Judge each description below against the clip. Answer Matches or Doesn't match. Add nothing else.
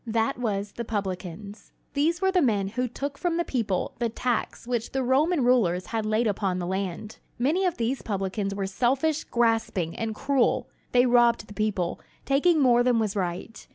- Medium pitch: Doesn't match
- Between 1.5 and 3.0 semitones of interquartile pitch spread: Doesn't match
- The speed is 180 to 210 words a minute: Matches